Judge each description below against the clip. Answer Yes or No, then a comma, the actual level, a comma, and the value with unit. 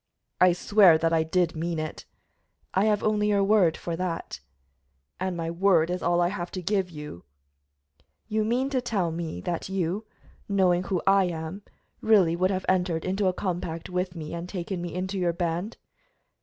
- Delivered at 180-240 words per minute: Yes, average, 185 wpm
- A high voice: No, medium, 180 Hz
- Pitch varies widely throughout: No, narrow, 2.6 semitones